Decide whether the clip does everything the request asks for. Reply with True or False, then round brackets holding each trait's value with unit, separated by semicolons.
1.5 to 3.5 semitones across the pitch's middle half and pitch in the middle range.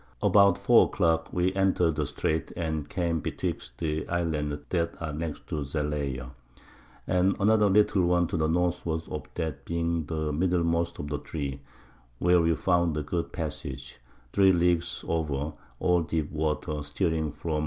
False (2.6 semitones; 80 Hz)